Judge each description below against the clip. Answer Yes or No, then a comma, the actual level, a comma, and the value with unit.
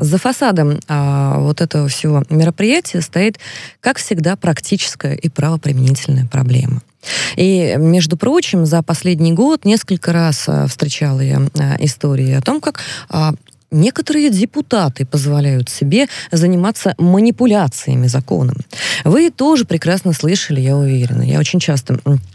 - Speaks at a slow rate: No, average, 125 wpm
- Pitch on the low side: No, medium, 155 Hz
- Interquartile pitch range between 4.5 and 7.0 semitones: Yes, average, 5.2 semitones